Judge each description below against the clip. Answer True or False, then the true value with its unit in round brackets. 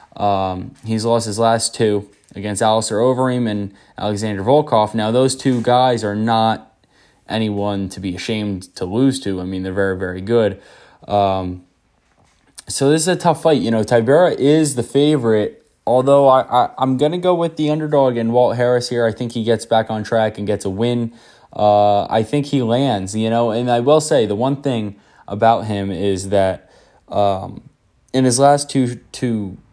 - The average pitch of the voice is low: True (115 Hz)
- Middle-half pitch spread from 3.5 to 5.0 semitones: True (4.0 semitones)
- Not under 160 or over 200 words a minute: True (190 wpm)